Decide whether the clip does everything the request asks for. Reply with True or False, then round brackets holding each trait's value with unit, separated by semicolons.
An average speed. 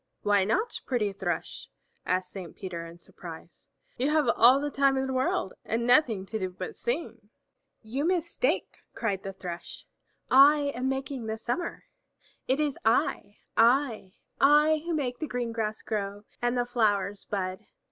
True (160 wpm)